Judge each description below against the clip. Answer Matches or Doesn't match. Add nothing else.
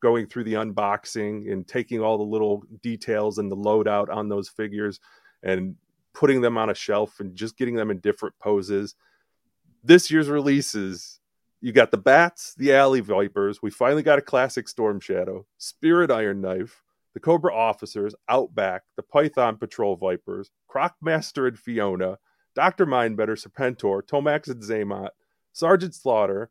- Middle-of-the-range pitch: Doesn't match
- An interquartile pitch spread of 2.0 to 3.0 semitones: Doesn't match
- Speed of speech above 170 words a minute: Doesn't match